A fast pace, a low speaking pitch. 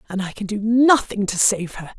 No: fast, 240 wpm; high, 210 Hz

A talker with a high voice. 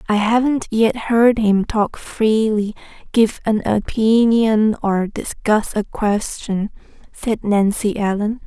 Yes: high, 215 Hz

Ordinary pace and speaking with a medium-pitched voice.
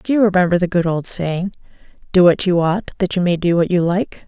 No: fast, 255 wpm; medium, 180 Hz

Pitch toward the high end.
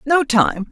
Yes: very high, 265 Hz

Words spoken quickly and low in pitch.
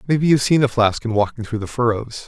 Yes: fast, 265 wpm; low, 120 Hz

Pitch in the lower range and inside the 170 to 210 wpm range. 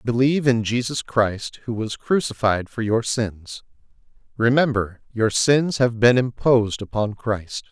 No: low, 115 Hz; average, 140 wpm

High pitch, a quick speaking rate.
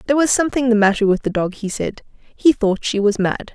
Yes: high, 225 Hz; fast, 255 wpm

